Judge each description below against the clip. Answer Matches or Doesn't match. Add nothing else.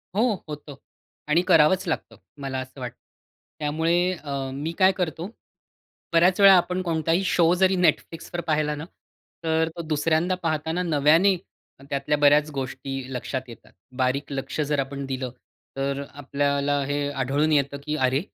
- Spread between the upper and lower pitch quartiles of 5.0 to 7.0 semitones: Doesn't match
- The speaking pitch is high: Doesn't match